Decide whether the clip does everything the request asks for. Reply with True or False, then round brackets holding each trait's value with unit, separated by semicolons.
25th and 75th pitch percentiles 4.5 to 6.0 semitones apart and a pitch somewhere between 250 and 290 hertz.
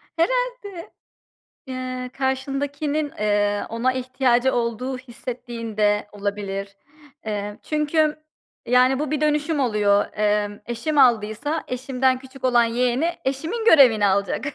True (5.1 semitones; 255 Hz)